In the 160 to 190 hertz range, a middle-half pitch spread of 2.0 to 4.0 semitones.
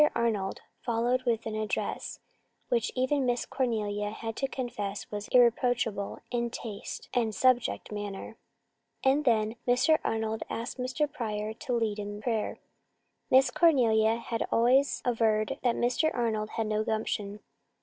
No: high, 230 Hz; narrow, 2.5 semitones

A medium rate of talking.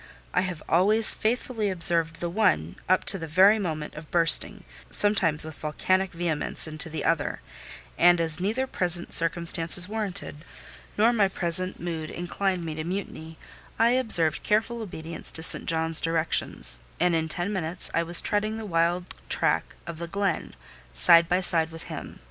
Yes: average, 165 wpm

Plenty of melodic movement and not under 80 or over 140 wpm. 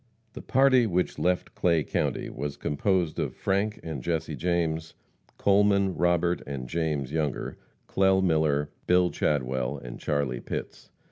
No: average, 4.0 semitones; slow, 135 wpm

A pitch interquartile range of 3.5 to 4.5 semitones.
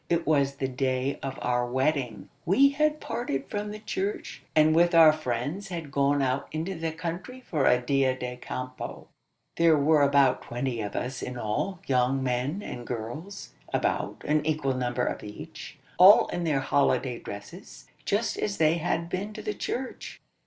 No: average, 5.2 semitones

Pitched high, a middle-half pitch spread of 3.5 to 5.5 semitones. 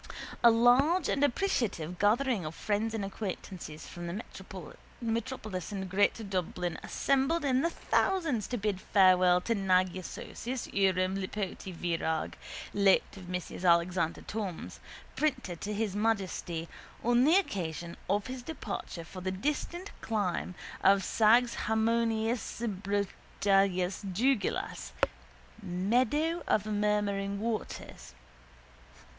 Yes: high, 205 Hz; average, 4.2 semitones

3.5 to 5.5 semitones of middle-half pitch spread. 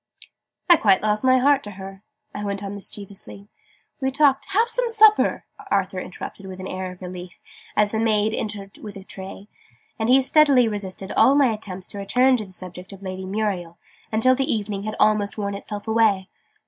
Yes: average, 4.2 semitones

